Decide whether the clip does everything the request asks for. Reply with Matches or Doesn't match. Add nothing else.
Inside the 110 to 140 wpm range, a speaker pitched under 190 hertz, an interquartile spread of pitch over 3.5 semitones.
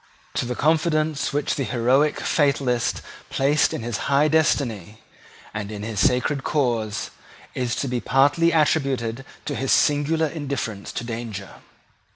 Matches